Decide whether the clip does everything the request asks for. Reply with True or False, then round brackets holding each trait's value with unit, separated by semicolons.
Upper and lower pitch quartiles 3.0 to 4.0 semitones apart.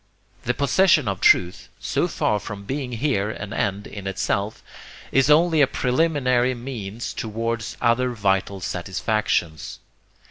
False (4.5 semitones)